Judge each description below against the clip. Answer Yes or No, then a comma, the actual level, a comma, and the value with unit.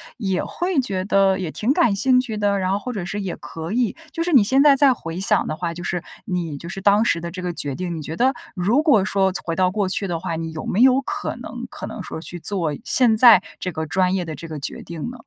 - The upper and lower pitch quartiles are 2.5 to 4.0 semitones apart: No, wide, 5.4 semitones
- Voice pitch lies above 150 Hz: Yes, high, 190 Hz